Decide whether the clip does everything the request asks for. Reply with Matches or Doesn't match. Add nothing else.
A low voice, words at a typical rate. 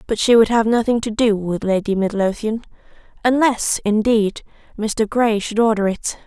Doesn't match